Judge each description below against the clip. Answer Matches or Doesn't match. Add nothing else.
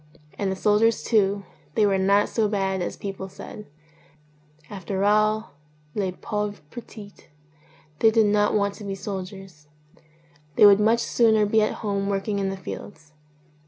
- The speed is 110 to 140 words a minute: Doesn't match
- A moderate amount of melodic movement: Doesn't match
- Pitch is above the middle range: Matches